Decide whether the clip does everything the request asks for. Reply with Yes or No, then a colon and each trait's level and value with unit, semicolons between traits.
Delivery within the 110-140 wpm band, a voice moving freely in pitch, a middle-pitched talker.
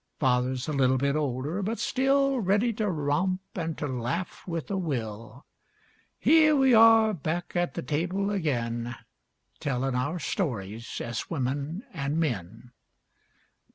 Yes: slow, 135 wpm; wide, 7.3 semitones; medium, 150 Hz